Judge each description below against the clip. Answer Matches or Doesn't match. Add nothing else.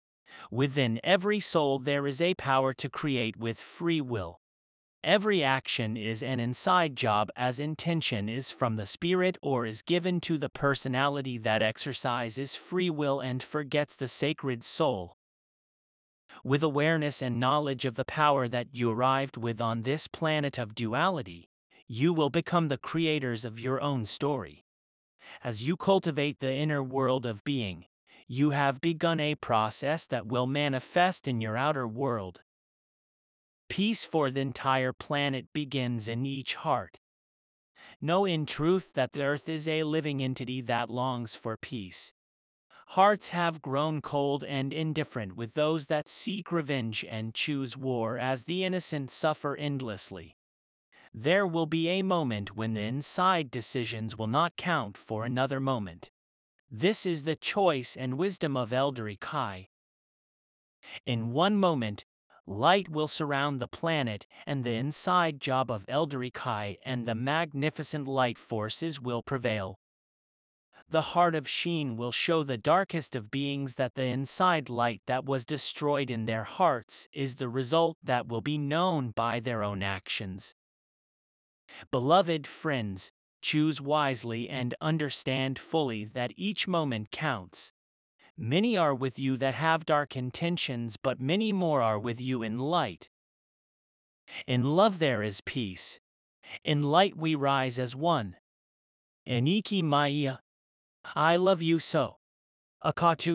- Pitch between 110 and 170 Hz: Matches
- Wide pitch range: Doesn't match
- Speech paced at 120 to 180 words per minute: Matches